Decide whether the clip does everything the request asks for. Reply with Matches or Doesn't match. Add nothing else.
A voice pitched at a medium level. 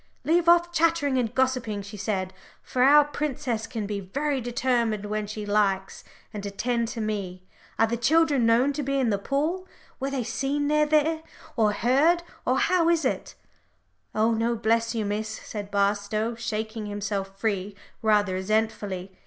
Doesn't match